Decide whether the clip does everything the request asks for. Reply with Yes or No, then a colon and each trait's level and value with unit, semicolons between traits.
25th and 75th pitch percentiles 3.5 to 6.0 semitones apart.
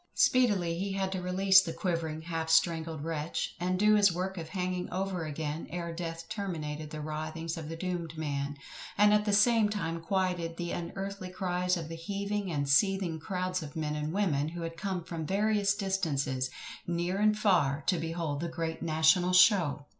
No: average, 3.1 semitones